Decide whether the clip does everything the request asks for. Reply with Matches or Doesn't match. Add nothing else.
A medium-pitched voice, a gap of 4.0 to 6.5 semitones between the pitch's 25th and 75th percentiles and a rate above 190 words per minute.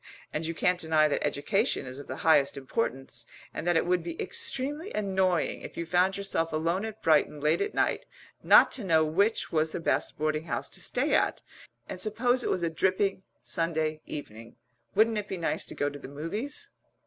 Matches